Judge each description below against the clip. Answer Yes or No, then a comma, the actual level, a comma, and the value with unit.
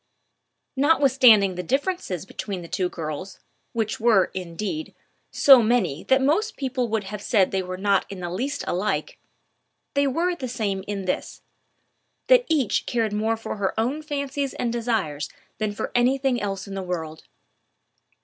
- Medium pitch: No, high, 220 Hz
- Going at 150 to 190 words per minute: Yes, average, 160 wpm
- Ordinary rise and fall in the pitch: No, wide, 5.9 semitones